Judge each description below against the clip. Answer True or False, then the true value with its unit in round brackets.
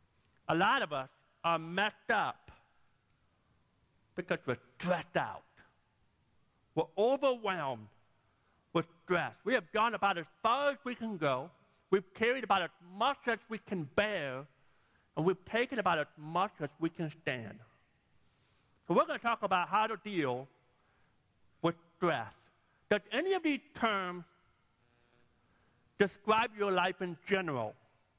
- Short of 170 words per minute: True (140 wpm)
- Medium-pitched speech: True (180 Hz)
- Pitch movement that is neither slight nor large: False (7.7 semitones)